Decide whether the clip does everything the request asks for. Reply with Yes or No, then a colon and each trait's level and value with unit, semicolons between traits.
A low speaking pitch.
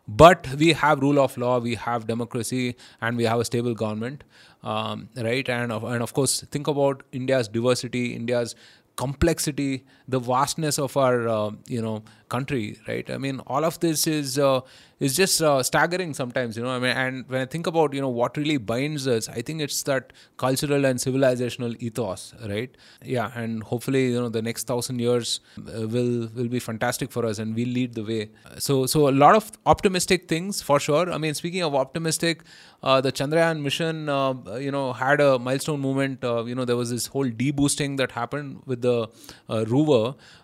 Yes: low, 130 Hz